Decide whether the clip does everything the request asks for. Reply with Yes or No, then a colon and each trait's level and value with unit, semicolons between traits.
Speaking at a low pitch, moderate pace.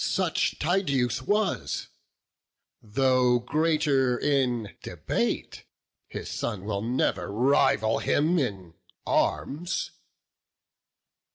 No: low, 130 Hz; slow, 80 wpm